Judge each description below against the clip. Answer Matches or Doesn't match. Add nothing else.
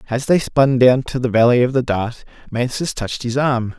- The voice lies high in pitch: Doesn't match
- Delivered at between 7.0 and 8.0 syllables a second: Doesn't match